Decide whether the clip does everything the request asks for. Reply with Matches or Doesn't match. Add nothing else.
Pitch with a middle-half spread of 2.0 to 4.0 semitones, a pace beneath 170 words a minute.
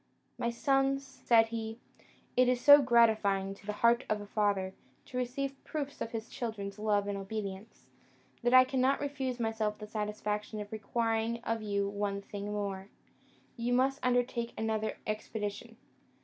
Matches